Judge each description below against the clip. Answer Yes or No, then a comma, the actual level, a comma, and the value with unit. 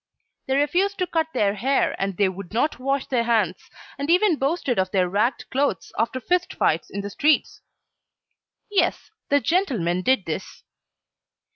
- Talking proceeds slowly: No, average, 160 wpm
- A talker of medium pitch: No, very high, 260 Hz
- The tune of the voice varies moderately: No, wide, 7.4 semitones